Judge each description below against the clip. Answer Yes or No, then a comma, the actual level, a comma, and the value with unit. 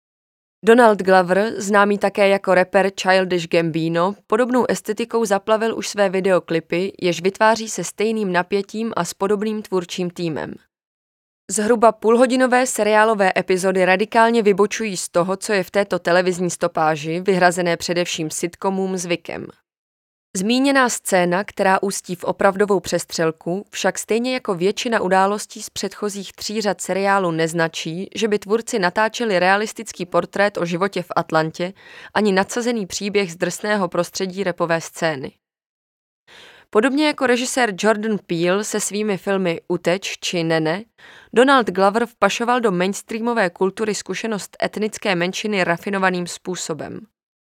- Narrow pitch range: No, average, 3.3 semitones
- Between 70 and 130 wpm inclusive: Yes, average, 125 wpm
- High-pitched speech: Yes, high, 195 Hz